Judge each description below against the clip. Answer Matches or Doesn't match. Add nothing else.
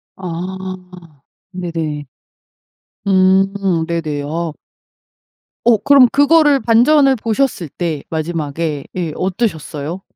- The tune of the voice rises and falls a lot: Matches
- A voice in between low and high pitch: Matches